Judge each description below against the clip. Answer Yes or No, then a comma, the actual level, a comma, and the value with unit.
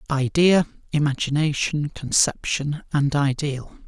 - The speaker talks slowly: Yes, slow, 75 wpm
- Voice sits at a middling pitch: Yes, medium, 145 Hz